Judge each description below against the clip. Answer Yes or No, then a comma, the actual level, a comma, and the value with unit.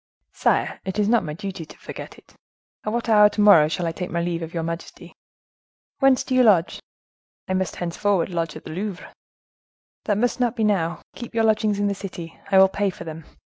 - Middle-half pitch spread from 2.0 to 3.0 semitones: No, average, 4.0 semitones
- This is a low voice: No, high, 195 Hz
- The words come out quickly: Yes, fast, 210 wpm